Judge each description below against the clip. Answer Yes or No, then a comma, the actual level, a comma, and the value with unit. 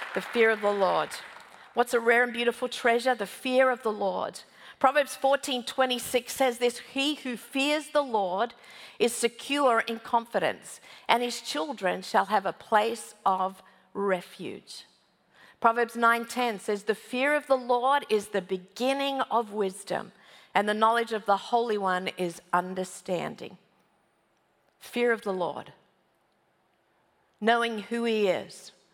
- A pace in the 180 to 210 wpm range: No, average, 140 wpm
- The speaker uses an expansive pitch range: No, average, 3.6 semitones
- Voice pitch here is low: No, high, 235 Hz